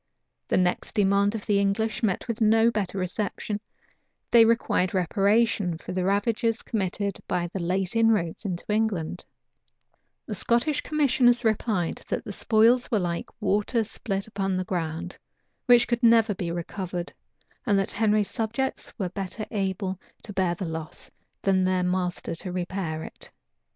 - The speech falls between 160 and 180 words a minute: No, average, 150 wpm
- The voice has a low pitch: No, high, 200 Hz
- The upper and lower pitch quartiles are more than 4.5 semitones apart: No, average, 3.5 semitones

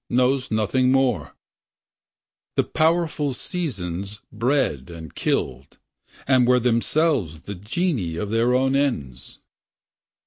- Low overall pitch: Yes, low, 125 Hz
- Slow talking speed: Yes, slow, 105 wpm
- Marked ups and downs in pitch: Yes, wide, 6.2 semitones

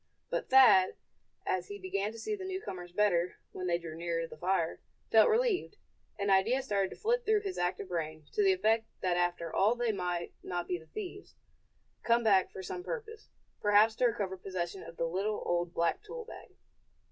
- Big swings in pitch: Yes, wide, 5.8 semitones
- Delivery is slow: No, average, 195 wpm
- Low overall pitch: No, high, 195 Hz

